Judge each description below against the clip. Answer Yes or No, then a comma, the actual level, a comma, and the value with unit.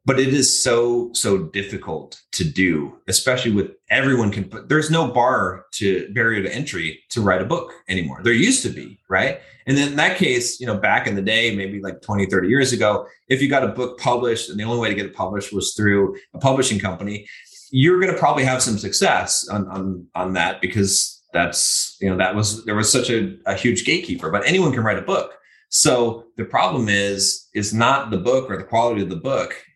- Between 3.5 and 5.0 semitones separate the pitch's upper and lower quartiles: Yes, average, 4.6 semitones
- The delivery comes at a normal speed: No, fast, 220 wpm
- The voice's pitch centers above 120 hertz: No, low, 110 Hz